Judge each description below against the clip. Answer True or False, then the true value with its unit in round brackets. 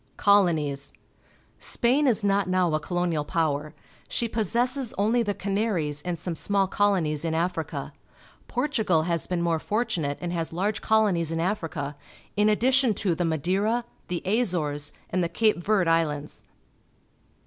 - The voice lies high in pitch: False (180 Hz)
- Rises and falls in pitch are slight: False (4.6 semitones)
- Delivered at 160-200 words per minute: False (150 wpm)